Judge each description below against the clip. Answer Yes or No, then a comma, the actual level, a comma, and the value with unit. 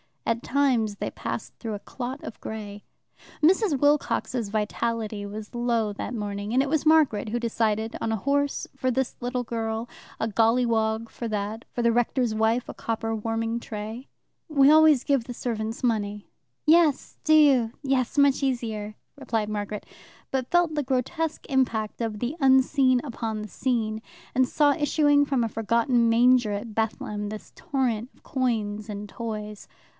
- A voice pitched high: Yes, high, 235 Hz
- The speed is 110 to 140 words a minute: No, average, 160 wpm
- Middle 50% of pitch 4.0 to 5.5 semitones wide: No, average, 3.4 semitones